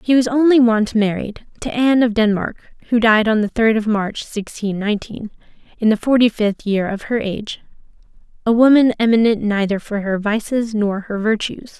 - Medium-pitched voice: No, high, 220 Hz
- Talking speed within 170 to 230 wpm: Yes, average, 185 wpm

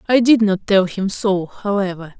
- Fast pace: No, average, 190 wpm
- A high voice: Yes, high, 200 Hz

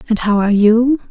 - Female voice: Yes, female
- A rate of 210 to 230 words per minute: Yes, fast, 215 wpm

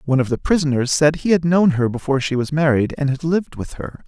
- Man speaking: Yes, male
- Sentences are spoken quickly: Yes, fast, 265 wpm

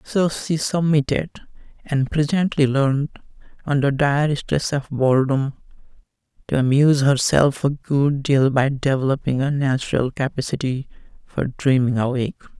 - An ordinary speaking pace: No, slow, 120 wpm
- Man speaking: Yes, male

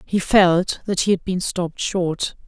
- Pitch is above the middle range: No, medium, 180 Hz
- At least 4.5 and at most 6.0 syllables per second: No, 4.1 syllables/s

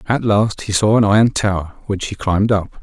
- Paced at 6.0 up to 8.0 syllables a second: No, 5.4 syllables/s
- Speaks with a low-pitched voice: Yes, low, 100 Hz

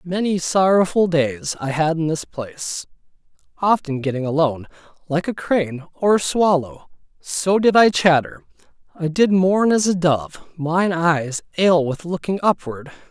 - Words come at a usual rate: Yes, average, 150 wpm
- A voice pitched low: No, medium, 165 Hz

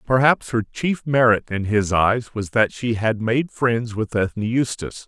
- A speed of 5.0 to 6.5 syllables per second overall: No, 4.4 syllables/s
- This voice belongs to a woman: No, male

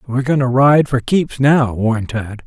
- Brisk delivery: Yes, fast, 220 wpm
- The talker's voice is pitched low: Yes, low, 130 Hz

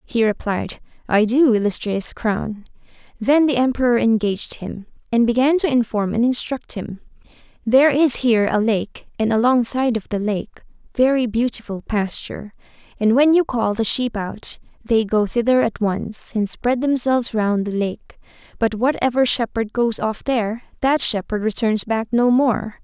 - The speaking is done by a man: No, female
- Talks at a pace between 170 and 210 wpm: No, average, 160 wpm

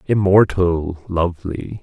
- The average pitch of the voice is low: Yes, very low, 90 Hz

